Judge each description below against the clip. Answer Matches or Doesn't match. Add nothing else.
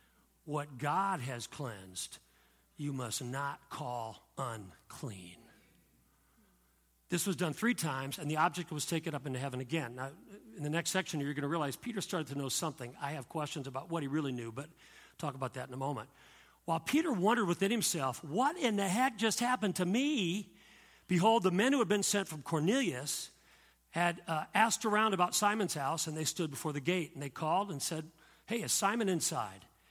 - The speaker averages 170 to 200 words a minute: Matches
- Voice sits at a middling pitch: Matches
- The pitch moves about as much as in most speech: Doesn't match